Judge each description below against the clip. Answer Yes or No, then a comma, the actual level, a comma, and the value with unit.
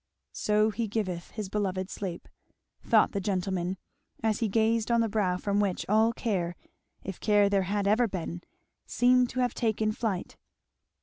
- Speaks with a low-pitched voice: No, high, 205 Hz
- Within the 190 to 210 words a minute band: No, average, 165 wpm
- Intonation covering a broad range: No, average, 2.9 semitones